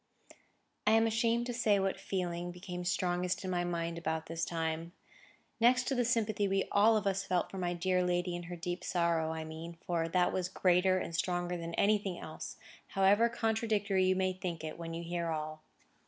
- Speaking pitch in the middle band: Yes, medium, 180 Hz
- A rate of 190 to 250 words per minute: Yes, average, 200 wpm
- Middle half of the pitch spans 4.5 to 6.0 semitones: No, average, 2.8 semitones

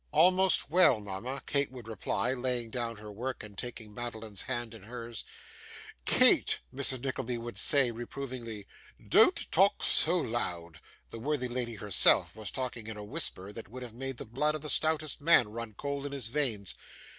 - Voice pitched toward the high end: No, low, 120 Hz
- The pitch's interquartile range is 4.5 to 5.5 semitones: No, average, 3.8 semitones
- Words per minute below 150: No, average, 170 wpm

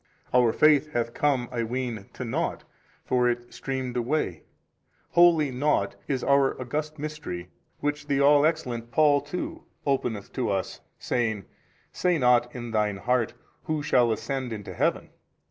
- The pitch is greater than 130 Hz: No, low, 125 Hz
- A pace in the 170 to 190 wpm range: No, average, 145 wpm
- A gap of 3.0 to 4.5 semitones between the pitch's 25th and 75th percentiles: Yes, average, 3.7 semitones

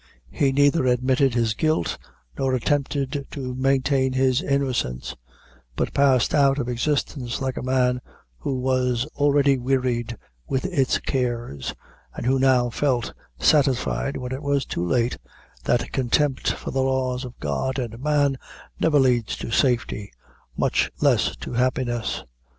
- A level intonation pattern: Yes, narrow, 2.0 semitones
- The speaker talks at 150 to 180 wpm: No, average, 140 wpm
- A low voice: Yes, low, 130 Hz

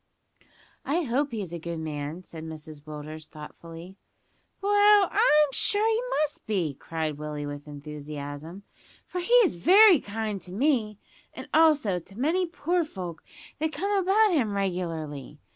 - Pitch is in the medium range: No, high, 195 Hz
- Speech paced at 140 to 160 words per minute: Yes, average, 145 wpm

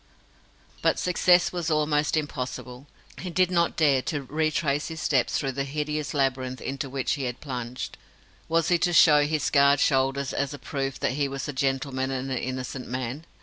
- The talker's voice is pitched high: No, medium, 140 Hz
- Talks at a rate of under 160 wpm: No, average, 185 wpm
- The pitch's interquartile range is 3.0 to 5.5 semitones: No, narrow, 2.6 semitones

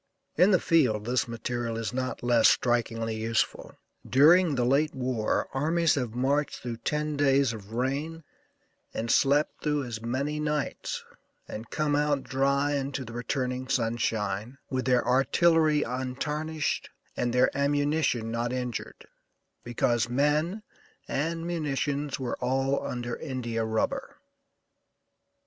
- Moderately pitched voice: No, low, 130 Hz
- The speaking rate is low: Yes, slow, 125 wpm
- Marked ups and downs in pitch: No, average, 3.7 semitones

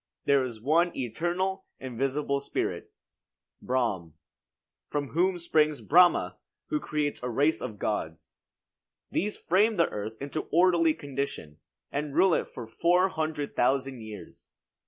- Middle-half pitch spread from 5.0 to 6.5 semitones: Yes, average, 5.3 semitones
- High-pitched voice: No, medium, 145 Hz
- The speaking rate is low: Yes, slow, 130 wpm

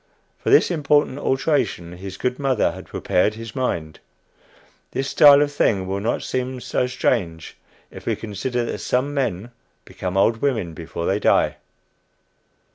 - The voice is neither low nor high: No, low, 120 Hz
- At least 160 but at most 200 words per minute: No, average, 150 wpm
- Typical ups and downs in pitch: No, wide, 6.1 semitones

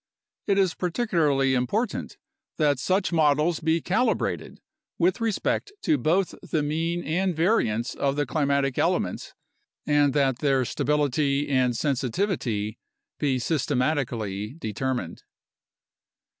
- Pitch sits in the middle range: Yes, medium, 145 Hz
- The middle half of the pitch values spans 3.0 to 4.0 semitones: No, average, 4.5 semitones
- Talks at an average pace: No, slow, 110 wpm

